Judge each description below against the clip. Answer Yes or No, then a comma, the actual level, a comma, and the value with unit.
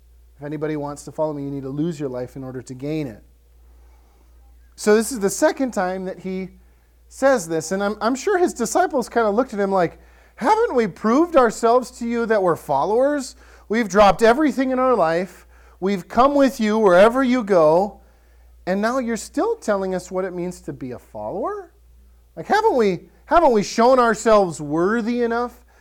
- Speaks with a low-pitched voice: No, high, 200 Hz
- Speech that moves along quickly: No, average, 195 wpm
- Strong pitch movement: Yes, wide, 8.0 semitones